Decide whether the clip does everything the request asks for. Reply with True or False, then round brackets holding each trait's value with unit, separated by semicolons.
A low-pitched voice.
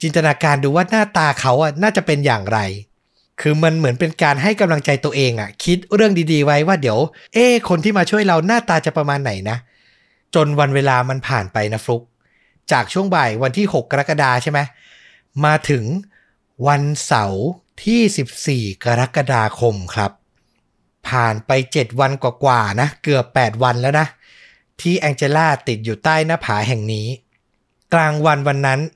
False (145 Hz)